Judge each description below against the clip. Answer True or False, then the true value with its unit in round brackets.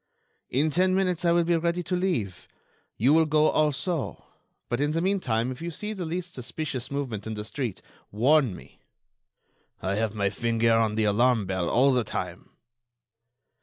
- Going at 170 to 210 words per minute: True (175 wpm)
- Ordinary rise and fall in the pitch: False (7.1 semitones)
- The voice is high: False (135 Hz)